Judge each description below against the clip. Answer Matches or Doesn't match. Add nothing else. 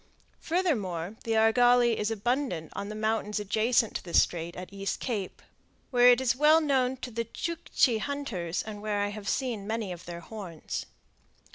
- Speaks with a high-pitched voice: Matches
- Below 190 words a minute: Matches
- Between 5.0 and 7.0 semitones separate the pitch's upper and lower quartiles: Doesn't match